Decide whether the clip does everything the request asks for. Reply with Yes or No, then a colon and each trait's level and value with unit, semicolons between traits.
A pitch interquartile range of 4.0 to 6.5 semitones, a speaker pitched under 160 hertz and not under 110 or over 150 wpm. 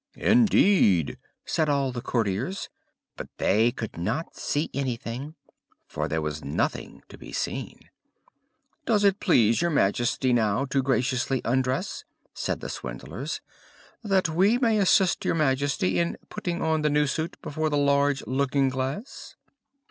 Yes: average, 5.2 semitones; medium, 140 Hz; average, 140 wpm